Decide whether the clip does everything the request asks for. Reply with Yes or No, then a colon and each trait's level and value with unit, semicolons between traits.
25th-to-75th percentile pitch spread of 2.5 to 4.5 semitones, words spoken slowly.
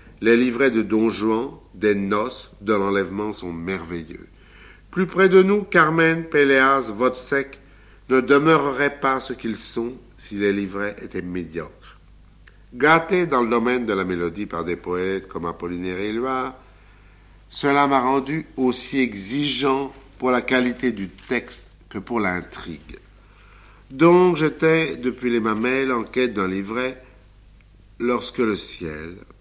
No: wide, 5.6 semitones; slow, 140 wpm